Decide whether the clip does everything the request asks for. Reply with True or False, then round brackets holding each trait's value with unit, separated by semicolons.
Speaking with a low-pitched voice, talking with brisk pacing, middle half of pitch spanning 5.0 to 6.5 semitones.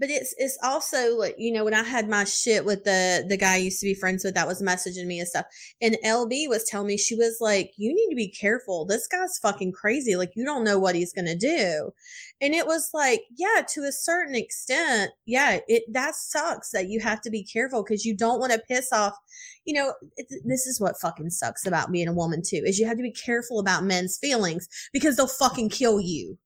False (225 Hz; 245 wpm; 5.4 semitones)